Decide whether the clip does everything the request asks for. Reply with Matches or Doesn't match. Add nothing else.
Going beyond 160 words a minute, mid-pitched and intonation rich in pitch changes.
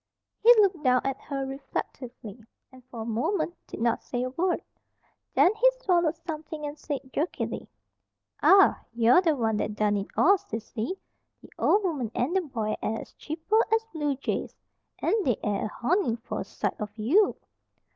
Doesn't match